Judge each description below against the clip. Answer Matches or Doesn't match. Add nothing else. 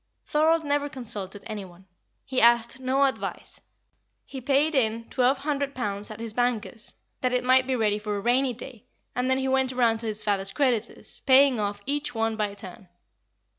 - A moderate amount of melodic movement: Matches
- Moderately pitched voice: Doesn't match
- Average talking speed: Matches